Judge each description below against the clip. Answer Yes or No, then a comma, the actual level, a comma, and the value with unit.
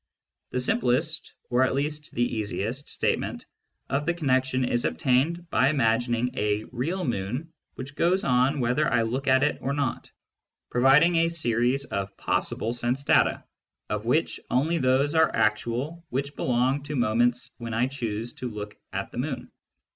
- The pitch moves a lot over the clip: No, average, 3.3 semitones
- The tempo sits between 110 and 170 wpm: Yes, average, 160 wpm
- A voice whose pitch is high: No, low, 130 Hz